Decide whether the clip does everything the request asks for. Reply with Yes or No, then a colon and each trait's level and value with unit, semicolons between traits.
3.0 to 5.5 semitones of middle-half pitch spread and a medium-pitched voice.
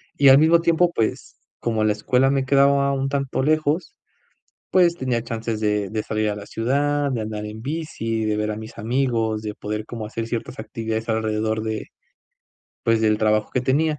No: average, 4.3 semitones; low, 115 Hz